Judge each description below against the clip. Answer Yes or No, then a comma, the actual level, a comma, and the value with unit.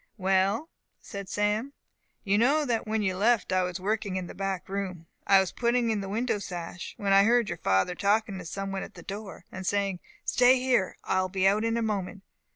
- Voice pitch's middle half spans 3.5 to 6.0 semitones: No, average, 2.9 semitones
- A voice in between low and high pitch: No, high, 200 Hz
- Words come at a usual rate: No, fast, 220 wpm